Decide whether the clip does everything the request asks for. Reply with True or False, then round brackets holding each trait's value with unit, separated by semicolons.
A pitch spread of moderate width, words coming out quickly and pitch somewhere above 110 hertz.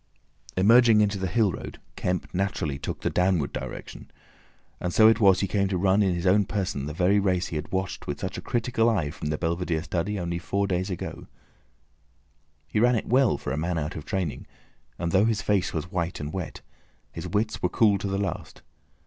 False (3.1 semitones; 210 wpm; 95 Hz)